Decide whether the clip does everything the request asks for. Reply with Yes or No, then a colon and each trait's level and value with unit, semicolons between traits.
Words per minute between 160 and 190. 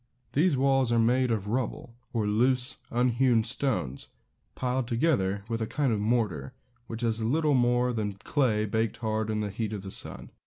Yes: average, 180 wpm